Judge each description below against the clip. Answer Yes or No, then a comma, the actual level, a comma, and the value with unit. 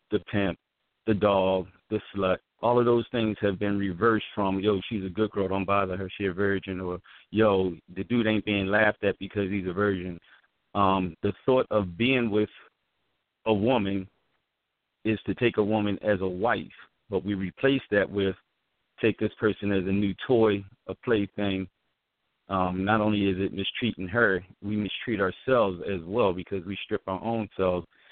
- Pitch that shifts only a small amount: Yes, narrow, 2.0 semitones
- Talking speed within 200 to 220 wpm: No, average, 180 wpm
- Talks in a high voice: No, low, 100 Hz